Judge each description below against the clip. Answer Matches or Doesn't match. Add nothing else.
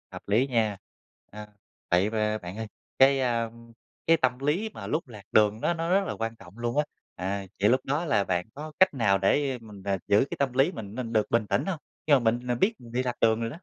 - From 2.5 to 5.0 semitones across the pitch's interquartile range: Matches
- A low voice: Matches